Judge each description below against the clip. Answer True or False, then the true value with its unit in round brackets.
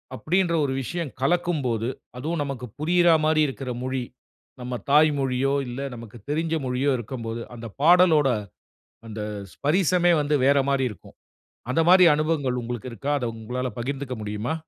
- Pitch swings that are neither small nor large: True (4.2 semitones)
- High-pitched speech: False (135 Hz)